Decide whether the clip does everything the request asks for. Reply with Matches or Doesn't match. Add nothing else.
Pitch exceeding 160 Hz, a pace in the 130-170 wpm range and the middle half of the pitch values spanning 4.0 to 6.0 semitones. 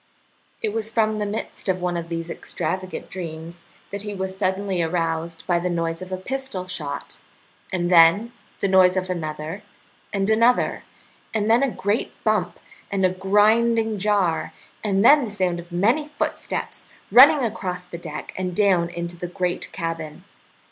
Doesn't match